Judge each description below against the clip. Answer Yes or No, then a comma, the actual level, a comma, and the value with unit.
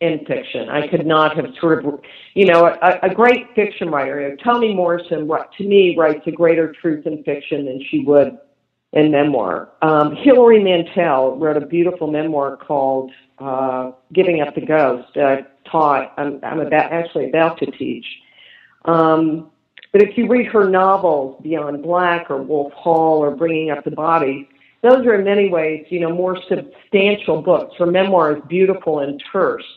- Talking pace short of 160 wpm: No, average, 180 wpm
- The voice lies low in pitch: No, medium, 160 Hz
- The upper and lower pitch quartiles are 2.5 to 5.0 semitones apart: Yes, average, 3.7 semitones